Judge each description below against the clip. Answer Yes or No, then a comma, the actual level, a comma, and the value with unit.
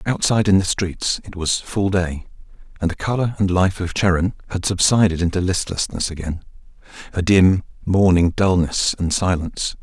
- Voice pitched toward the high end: No, very low, 90 Hz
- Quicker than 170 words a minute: No, average, 160 wpm